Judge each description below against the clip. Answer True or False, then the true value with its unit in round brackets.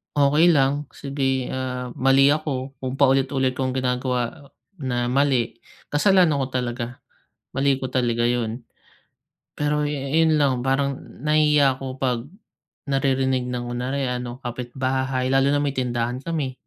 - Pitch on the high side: False (130 Hz)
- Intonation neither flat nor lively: False (2.0 semitones)